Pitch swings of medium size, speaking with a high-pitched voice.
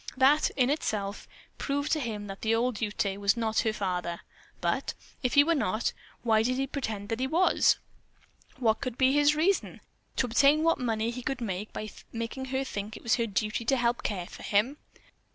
Yes: average, 4.0 semitones; high, 235 Hz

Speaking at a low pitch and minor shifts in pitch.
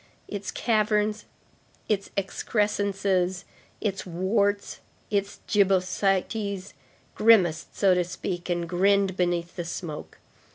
No: high, 195 Hz; narrow, 2.2 semitones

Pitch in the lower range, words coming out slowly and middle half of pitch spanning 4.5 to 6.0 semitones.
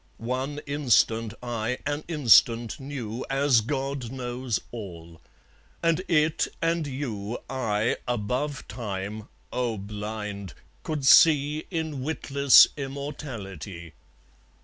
Yes: low, 125 Hz; slow, 100 wpm; average, 4.9 semitones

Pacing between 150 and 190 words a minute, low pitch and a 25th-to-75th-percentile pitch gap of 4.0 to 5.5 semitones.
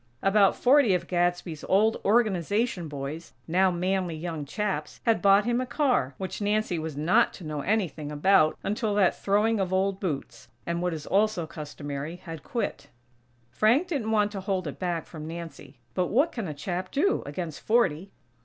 No: average, 175 wpm; medium, 185 Hz; average, 4.6 semitones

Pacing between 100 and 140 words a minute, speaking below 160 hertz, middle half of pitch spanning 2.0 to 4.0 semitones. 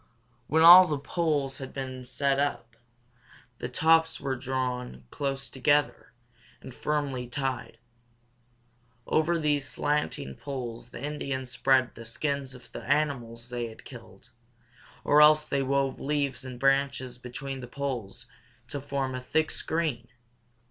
Yes: slow, 135 wpm; low, 135 Hz; narrow, 2.6 semitones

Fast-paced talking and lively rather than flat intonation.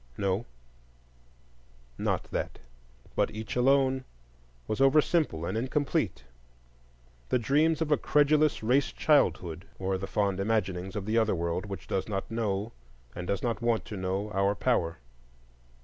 No: average, 140 wpm; wide, 5.8 semitones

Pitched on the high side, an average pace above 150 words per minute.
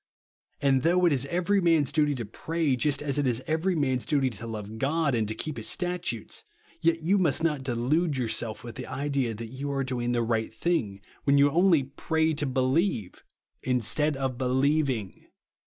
No: low, 135 Hz; average, 190 wpm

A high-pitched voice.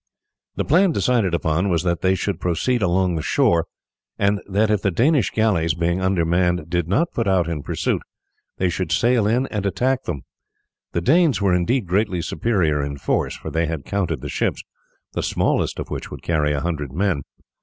No: very low, 90 Hz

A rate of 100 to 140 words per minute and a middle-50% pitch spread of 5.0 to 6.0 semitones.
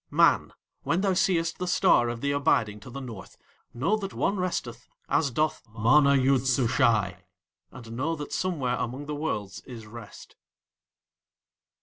No: average, 150 wpm; average, 5.3 semitones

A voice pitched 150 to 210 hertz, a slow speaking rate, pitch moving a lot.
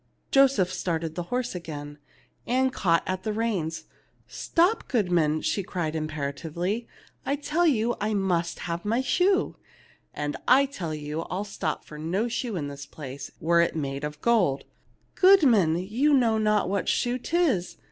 No: medium, 185 Hz; average, 160 wpm; wide, 7.2 semitones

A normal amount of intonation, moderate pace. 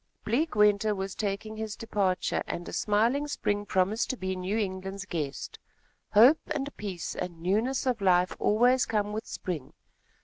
Yes: average, 3.2 semitones; average, 160 wpm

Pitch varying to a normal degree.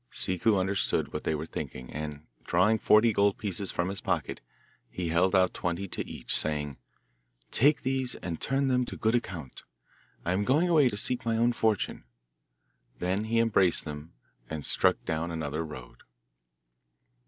No: wide, 5.7 semitones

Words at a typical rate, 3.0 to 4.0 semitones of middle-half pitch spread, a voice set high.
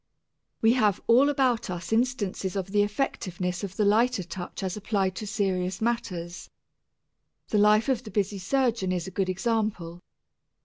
Yes: average, 160 wpm; average, 3.6 semitones; high, 205 Hz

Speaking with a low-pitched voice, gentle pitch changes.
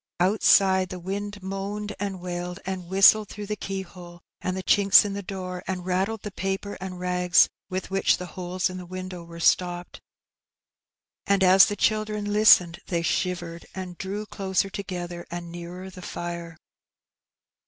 No: medium, 185 Hz; narrow, 1.8 semitones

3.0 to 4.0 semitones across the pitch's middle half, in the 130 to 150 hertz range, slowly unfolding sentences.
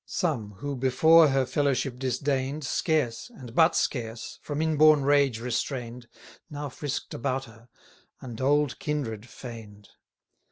Yes: average, 3.5 semitones; low, 135 Hz; slow, 130 wpm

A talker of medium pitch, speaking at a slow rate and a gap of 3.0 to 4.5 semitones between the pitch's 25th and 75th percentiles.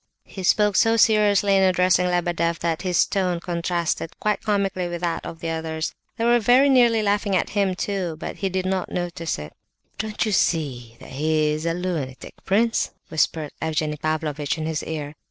No: medium, 175 Hz; average, 180 wpm; average, 3.9 semitones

